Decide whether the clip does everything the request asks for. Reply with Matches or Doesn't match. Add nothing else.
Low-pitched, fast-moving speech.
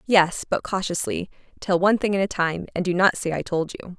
Doesn't match